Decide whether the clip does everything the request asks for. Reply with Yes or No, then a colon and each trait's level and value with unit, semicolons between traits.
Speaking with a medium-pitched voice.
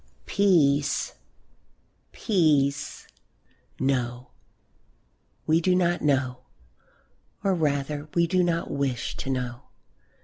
Yes: medium, 145 Hz